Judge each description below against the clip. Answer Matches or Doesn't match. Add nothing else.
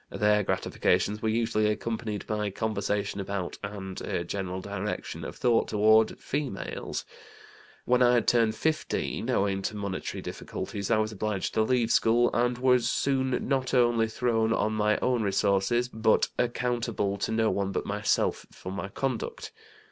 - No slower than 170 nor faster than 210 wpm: Doesn't match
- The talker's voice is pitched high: Doesn't match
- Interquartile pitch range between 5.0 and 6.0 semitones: Doesn't match